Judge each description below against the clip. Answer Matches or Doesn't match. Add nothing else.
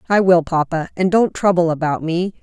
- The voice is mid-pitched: Matches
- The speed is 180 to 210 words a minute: Matches